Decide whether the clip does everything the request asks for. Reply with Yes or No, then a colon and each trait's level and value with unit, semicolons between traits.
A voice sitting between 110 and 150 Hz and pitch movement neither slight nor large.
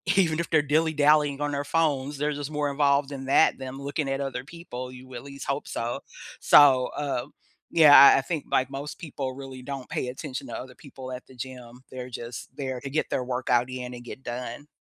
No: low, 135 Hz; narrow, 2.3 semitones